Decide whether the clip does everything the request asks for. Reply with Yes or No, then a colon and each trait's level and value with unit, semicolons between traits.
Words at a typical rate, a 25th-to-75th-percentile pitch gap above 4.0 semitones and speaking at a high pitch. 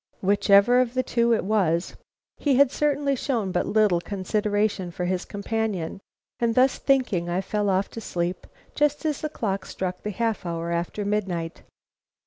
Yes: average, 165 wpm; average, 4.5 semitones; high, 205 Hz